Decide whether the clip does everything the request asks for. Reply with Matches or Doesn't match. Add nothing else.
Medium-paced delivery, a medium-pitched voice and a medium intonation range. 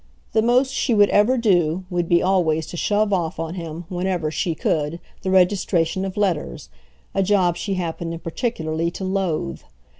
Matches